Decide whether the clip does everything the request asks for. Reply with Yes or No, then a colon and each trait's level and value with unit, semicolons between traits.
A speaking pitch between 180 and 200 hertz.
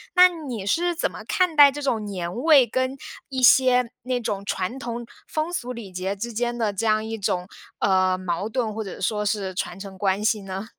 No: high, 220 Hz